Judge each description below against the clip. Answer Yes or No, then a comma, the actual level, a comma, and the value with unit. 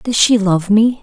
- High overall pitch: Yes, high, 210 Hz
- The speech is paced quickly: Yes, fast, 235 wpm